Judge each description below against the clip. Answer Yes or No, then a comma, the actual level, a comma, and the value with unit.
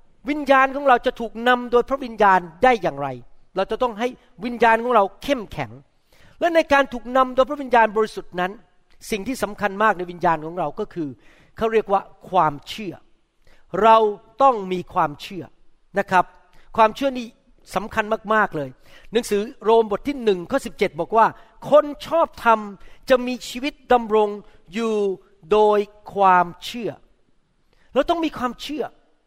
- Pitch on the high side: Yes, high, 220 Hz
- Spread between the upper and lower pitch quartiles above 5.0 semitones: Yes, wide, 5.4 semitones